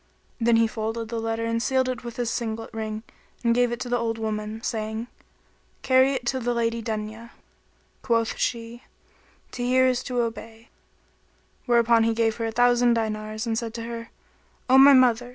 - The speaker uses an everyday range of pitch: No, narrow, 1.4 semitones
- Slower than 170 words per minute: No, average, 185 wpm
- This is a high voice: Yes, high, 230 Hz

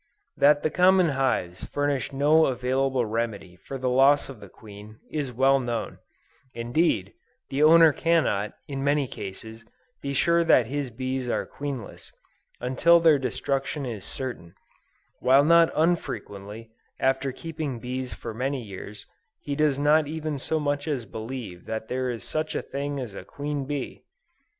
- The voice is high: No, low, 135 Hz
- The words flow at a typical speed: Yes, average, 155 wpm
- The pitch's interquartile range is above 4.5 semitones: No, average, 4.0 semitones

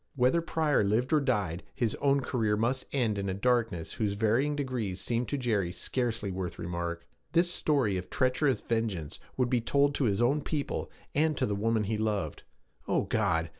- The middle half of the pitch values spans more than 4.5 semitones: Yes, average, 5.2 semitones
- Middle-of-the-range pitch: No, low, 115 Hz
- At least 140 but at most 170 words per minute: No, average, 185 wpm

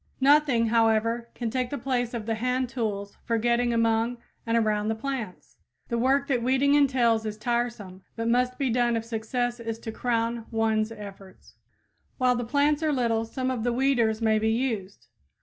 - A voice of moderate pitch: No, high, 235 Hz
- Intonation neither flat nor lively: No, narrow, 2.1 semitones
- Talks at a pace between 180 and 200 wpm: Yes, average, 185 wpm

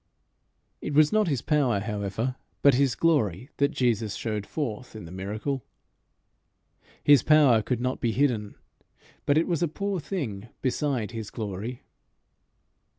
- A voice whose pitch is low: Yes, low, 125 Hz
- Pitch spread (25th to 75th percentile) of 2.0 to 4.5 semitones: No, wide, 5.4 semitones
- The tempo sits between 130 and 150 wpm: Yes, average, 145 wpm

